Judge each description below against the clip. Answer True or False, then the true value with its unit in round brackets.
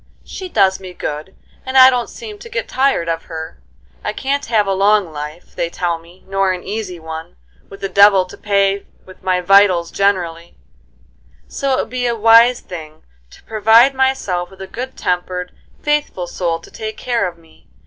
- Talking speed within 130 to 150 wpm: False (190 wpm)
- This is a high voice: True (195 Hz)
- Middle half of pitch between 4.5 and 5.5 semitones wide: True (4.9 semitones)